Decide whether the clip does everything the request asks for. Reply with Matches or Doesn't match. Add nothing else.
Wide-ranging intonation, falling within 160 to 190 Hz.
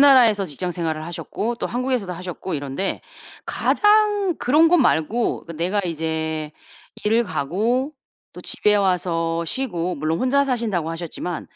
Matches